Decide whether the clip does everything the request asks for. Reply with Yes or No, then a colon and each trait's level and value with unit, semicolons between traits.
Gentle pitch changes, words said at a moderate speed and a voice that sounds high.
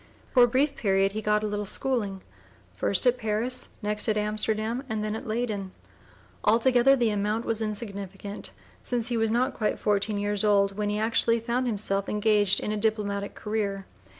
Yes: narrow, 2.1 semitones; average, 180 wpm; high, 215 Hz